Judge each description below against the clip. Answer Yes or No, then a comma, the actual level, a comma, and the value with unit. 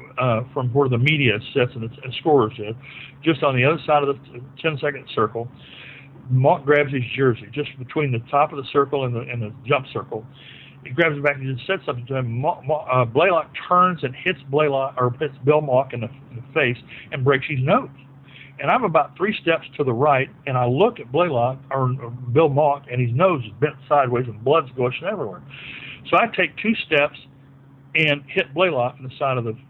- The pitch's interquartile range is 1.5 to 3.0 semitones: Yes, average, 2.7 semitones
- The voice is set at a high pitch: No, low, 135 Hz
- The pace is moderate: No, fast, 220 wpm